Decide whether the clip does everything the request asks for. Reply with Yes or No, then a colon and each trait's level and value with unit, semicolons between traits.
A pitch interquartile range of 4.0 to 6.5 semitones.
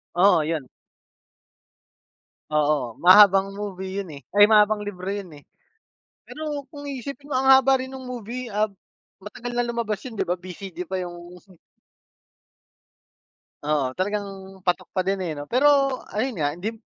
Yes: wide, 5.4 semitones